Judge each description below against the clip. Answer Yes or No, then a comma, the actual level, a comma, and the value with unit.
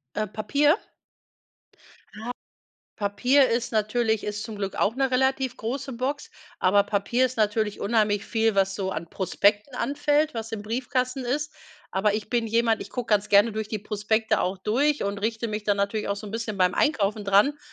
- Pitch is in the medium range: No, high, 220 Hz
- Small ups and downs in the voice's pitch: No, average, 3.5 semitones